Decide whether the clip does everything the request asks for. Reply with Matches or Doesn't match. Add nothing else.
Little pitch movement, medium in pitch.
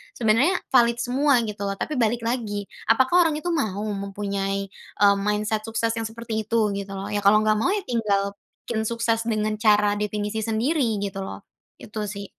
Doesn't match